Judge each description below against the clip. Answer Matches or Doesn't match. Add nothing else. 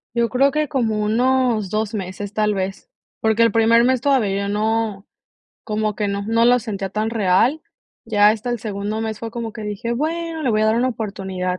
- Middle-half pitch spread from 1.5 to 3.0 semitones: Matches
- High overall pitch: Matches